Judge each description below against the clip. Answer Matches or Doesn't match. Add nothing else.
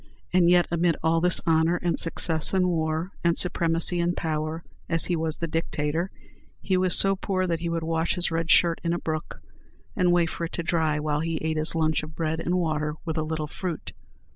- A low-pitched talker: Doesn't match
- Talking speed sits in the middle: Doesn't match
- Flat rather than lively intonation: Matches